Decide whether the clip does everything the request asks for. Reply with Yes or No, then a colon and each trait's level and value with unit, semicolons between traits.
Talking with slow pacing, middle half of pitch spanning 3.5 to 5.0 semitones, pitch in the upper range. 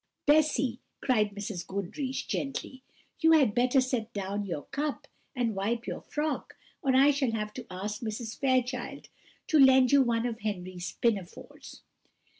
No: average, 150 wpm; average, 4.4 semitones; high, 240 Hz